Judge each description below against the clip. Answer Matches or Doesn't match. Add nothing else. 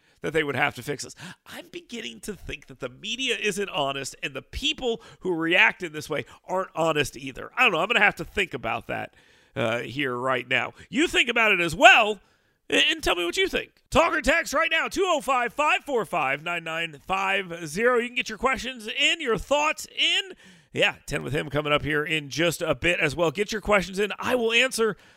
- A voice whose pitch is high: Matches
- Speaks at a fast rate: Matches